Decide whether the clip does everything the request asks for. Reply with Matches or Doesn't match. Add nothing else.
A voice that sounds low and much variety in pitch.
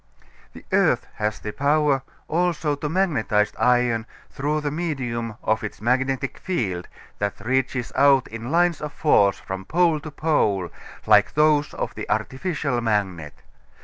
Matches